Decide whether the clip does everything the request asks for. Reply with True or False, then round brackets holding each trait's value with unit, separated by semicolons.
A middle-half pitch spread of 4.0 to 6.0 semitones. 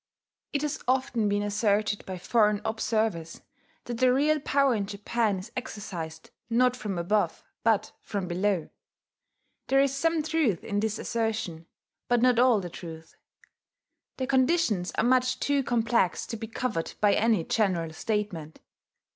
True (4.5 semitones)